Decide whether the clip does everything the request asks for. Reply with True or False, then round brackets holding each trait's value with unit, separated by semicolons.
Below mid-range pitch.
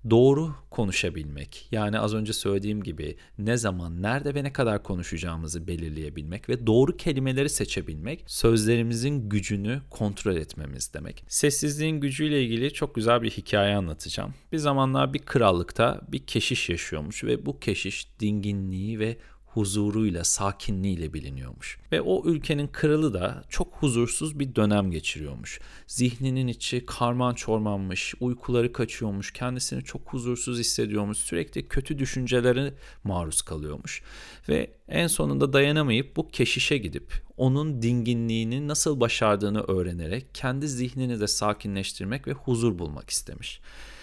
True (115 Hz)